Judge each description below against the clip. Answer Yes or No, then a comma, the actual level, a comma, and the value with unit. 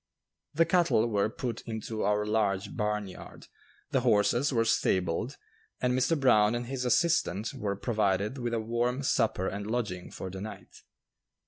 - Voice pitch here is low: Yes, low, 110 Hz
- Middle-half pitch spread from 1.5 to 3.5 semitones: Yes, average, 3.2 semitones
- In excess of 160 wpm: No, average, 150 wpm